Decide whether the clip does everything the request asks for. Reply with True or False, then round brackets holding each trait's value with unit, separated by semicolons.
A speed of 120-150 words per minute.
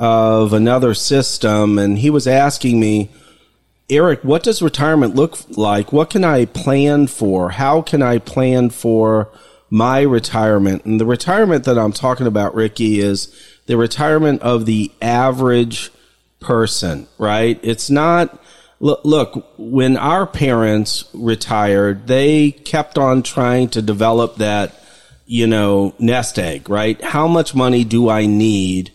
True (140 wpm)